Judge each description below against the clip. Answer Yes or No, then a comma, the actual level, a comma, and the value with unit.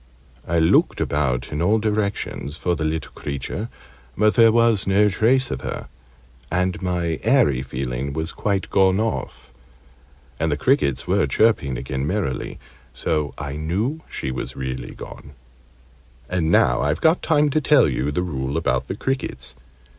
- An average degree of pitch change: No, wide, 7.5 semitones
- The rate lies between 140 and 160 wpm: Yes, average, 155 wpm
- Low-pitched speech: Yes, very low, 85 Hz